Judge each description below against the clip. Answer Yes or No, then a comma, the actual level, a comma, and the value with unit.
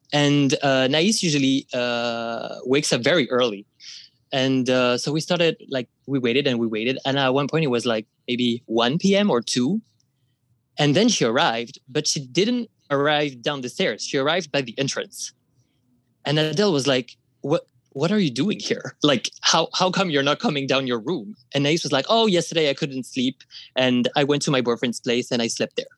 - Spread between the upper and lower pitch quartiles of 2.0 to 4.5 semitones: Yes, average, 3.7 semitones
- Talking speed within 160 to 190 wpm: No, fast, 205 wpm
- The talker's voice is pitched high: No, low, 135 Hz